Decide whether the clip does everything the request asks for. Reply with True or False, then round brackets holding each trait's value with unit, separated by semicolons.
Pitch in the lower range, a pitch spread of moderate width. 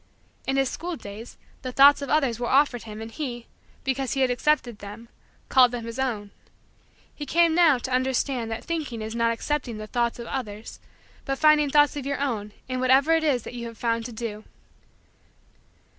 False (255 Hz; 3.4 semitones)